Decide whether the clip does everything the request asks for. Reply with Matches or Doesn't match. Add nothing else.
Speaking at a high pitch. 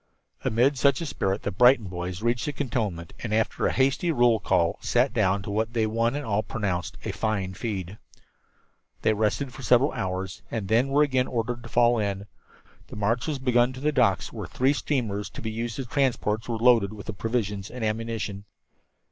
Doesn't match